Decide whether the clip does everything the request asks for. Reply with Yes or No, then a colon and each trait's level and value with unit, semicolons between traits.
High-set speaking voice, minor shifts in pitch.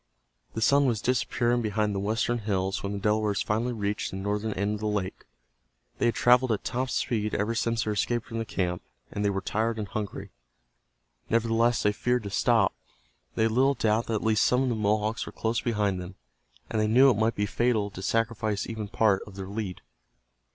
No: low, 110 Hz; narrow, 2.2 semitones